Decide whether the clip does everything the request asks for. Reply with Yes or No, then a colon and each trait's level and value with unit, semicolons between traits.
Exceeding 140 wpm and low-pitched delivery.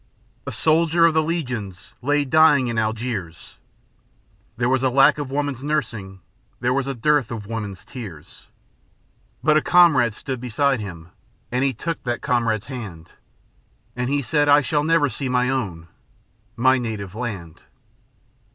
Yes: average, 150 wpm; low, 125 Hz